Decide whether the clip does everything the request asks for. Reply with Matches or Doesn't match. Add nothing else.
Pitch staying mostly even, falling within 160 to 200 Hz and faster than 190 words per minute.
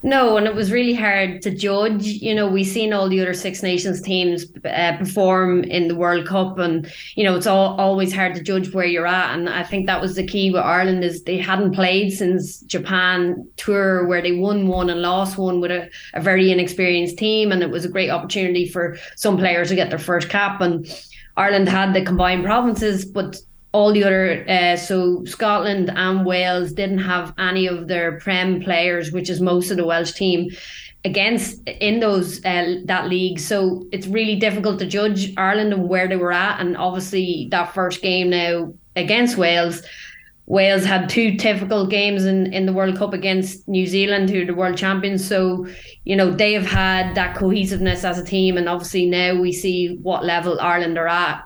Matches